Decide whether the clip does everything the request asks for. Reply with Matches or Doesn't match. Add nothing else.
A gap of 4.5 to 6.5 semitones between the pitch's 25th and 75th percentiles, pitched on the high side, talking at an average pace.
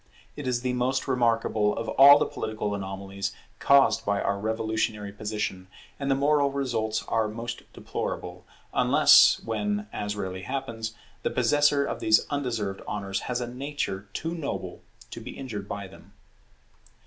Doesn't match